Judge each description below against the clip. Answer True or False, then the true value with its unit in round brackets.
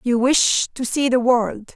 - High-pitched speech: True (245 Hz)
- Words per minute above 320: False (205 wpm)